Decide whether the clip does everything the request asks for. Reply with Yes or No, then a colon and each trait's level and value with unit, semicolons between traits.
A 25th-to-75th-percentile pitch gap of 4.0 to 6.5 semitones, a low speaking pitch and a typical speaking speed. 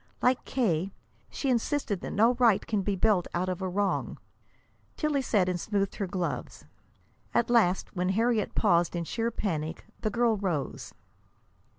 No: average, 4.4 semitones; high, 200 Hz; average, 160 wpm